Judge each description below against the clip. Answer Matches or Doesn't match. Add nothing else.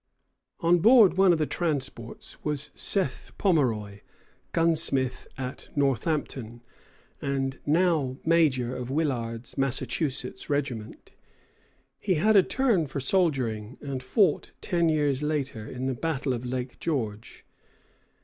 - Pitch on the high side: Doesn't match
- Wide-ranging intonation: Doesn't match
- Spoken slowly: Matches